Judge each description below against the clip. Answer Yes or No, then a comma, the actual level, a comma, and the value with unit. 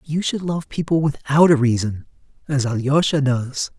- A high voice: No, medium, 145 Hz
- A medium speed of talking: Yes, average, 160 wpm